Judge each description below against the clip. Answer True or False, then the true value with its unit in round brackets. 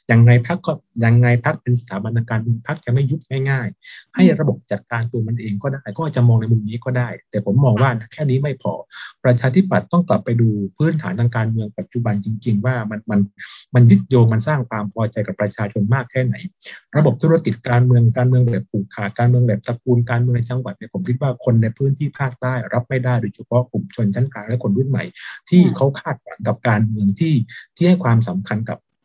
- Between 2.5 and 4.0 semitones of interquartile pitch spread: True (3.1 semitones)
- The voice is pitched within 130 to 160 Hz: False (120 Hz)